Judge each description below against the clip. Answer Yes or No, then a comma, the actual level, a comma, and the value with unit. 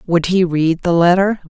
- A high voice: No, medium, 175 Hz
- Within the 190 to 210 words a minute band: Yes, average, 200 wpm